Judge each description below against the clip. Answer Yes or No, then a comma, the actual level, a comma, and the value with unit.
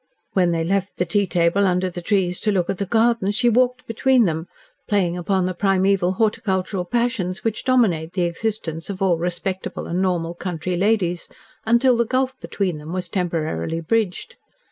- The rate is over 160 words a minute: Yes, average, 175 wpm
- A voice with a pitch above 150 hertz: Yes, medium, 185 Hz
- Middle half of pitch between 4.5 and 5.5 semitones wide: No, average, 3.9 semitones